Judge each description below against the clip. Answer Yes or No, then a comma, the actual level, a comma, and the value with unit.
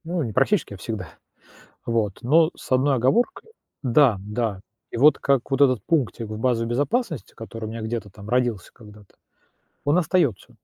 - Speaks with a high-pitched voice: No, low, 120 Hz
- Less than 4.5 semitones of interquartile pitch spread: No, average, 4.8 semitones